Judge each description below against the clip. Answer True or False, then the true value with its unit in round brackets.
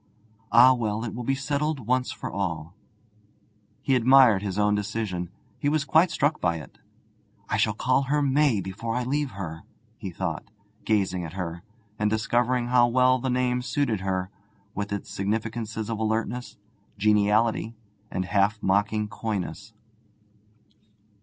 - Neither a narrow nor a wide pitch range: True (4.1 semitones)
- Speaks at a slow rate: False (145 wpm)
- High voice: False (110 Hz)